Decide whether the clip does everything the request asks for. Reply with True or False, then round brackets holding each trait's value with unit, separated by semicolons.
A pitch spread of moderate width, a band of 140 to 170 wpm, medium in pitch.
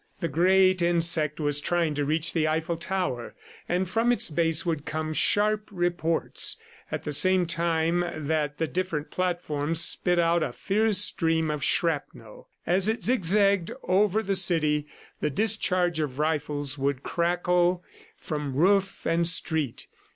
True (3.2 semitones; 145 wpm; 170 Hz)